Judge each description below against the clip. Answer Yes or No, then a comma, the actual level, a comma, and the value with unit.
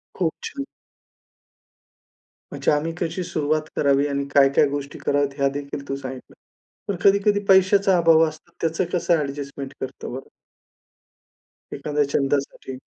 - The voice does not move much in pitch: No, average, 3.5 semitones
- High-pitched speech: No, medium, 145 Hz